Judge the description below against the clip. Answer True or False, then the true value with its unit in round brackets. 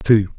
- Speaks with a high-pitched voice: False (105 Hz)